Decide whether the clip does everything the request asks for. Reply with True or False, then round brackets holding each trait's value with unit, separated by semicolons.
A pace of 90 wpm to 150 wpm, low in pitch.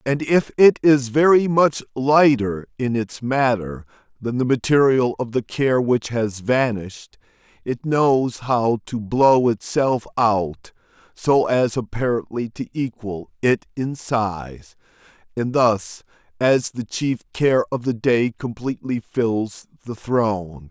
True (135 wpm; 120 Hz)